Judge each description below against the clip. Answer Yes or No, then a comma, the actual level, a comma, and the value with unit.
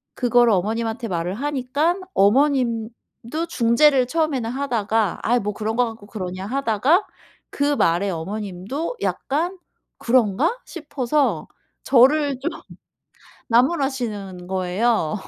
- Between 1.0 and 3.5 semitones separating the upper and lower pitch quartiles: No, average, 5.3 semitones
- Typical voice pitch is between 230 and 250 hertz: Yes, high, 240 Hz